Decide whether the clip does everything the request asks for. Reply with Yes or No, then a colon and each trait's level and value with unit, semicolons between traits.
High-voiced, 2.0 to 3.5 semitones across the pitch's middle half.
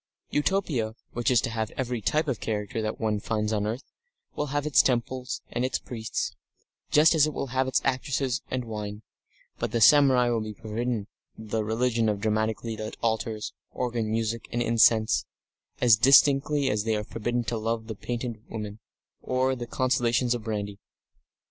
No: low, 115 Hz; average, 2.8 semitones